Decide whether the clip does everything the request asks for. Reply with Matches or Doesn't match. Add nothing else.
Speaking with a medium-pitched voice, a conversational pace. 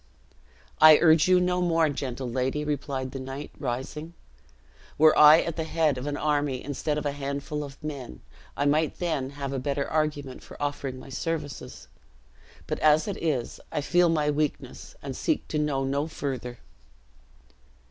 Matches